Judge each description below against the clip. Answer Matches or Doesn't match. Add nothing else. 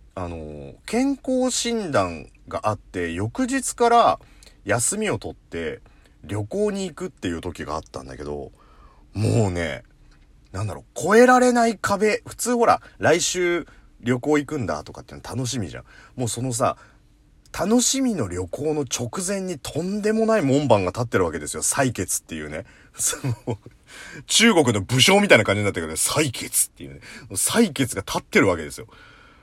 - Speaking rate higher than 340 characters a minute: Doesn't match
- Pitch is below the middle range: Matches